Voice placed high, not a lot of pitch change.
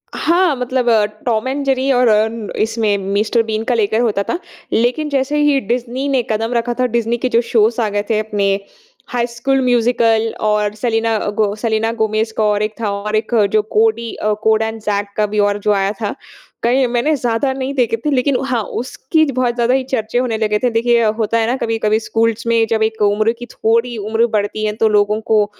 Yes: high, 225 Hz; narrow, 2.3 semitones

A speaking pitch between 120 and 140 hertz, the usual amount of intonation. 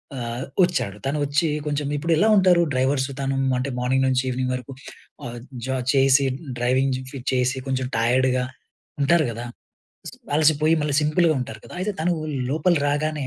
Yes: low, 135 Hz; average, 3.1 semitones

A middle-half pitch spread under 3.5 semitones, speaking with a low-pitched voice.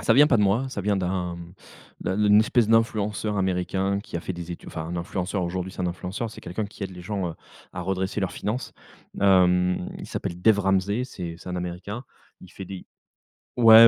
Yes: average, 2.9 semitones; very low, 95 Hz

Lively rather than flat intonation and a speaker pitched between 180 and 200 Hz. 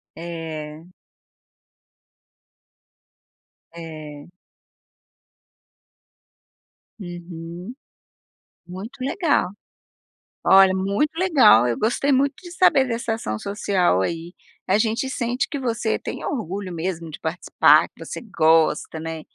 Yes: wide, 6.5 semitones; high, 190 Hz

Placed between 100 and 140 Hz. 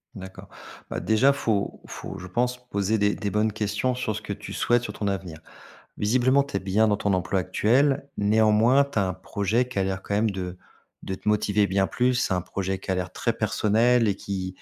Yes: low, 105 Hz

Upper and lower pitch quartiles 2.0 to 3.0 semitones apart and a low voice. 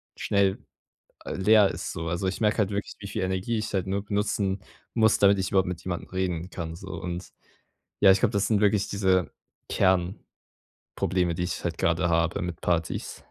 Yes: narrow, 2.4 semitones; very low, 95 Hz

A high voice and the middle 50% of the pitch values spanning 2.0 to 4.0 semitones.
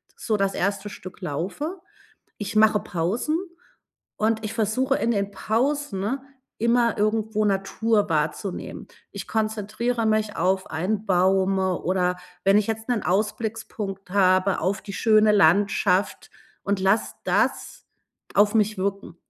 Yes: high, 205 Hz; narrow, 2.5 semitones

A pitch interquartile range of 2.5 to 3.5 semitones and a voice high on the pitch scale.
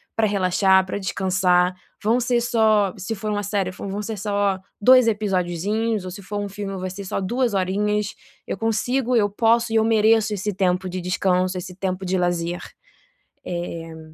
Yes: average, 2.8 semitones; high, 200 Hz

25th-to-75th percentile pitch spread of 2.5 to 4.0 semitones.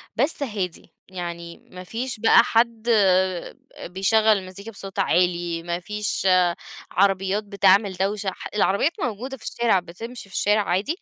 Yes: average, 3.7 semitones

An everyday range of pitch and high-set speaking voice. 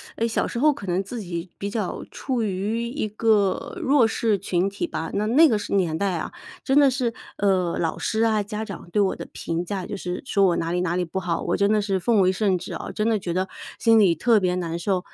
Yes: average, 3.7 semitones; high, 200 Hz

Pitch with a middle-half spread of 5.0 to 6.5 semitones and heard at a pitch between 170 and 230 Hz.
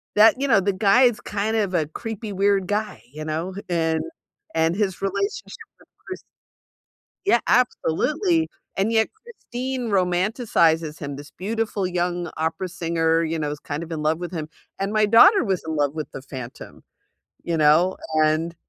Yes: wide, 5.4 semitones; medium, 185 Hz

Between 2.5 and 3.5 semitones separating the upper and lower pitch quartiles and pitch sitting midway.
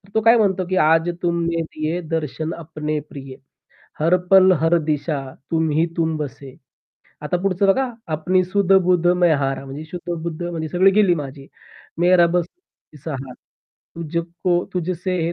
Yes: average, 2.9 semitones; medium, 170 Hz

